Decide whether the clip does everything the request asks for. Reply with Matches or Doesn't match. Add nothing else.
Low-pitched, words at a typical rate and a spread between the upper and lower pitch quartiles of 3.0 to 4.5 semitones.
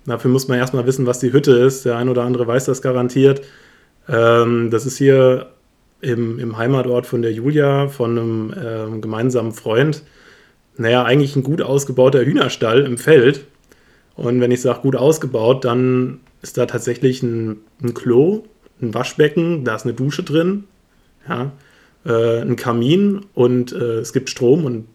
Doesn't match